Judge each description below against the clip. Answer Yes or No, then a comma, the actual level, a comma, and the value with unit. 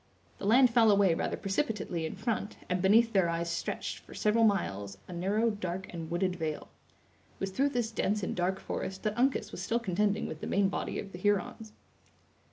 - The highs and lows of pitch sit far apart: No, average, 3.8 semitones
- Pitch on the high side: Yes, high, 195 Hz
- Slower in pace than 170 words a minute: No, average, 200 wpm